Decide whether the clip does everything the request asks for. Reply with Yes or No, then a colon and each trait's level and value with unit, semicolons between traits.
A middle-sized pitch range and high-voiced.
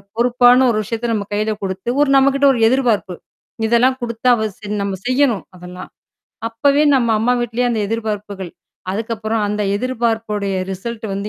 Yes: average, 3.0 semitones; high, 225 Hz